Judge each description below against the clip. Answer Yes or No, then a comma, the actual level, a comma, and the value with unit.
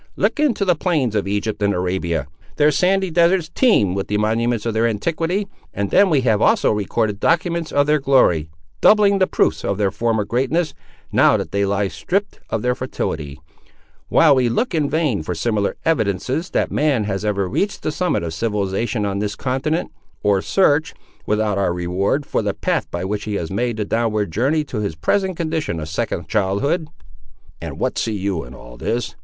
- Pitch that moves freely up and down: Yes, wide, 7.8 semitones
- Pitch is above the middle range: No, low, 115 Hz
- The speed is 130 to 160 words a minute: No, average, 190 wpm